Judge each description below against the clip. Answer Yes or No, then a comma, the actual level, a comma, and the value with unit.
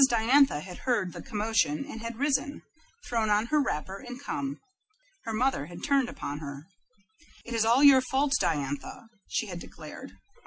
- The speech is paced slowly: No, average, 165 wpm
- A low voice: No, high, 230 Hz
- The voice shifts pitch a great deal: Yes, wide, 6.3 semitones